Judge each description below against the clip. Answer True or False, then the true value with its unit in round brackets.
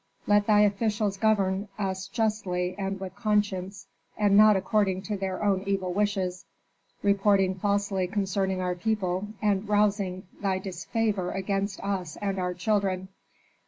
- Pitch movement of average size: False (1.7 semitones)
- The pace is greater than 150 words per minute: False (135 wpm)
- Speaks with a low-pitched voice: False (195 Hz)